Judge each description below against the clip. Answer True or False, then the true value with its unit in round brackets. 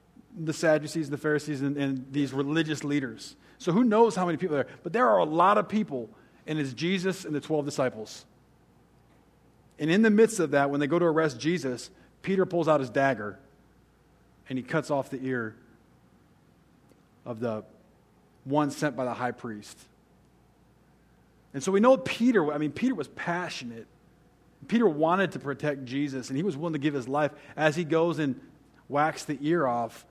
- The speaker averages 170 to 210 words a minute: True (185 wpm)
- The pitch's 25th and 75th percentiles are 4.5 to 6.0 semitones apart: False (4.1 semitones)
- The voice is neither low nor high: True (145 Hz)